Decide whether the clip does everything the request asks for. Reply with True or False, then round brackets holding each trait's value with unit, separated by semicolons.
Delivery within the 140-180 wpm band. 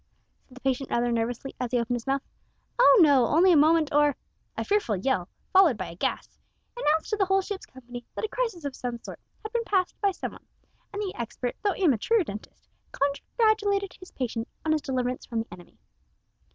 False (205 wpm)